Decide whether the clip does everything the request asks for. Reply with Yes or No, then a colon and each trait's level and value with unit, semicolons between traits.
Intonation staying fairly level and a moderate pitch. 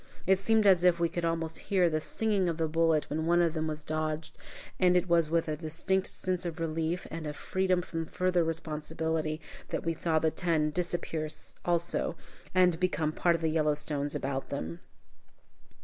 Yes: narrow, 2.2 semitones; medium, 165 Hz